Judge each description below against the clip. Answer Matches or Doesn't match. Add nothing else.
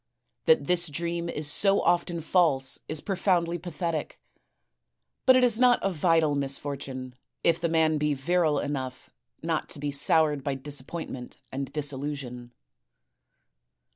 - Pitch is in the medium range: Matches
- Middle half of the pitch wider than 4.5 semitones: Doesn't match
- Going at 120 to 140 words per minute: Matches